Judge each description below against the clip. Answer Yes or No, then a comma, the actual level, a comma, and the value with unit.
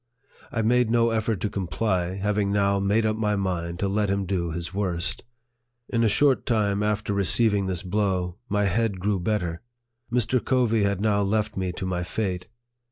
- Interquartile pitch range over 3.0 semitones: No, average, 2.7 semitones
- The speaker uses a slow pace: No, average, 180 wpm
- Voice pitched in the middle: No, low, 100 Hz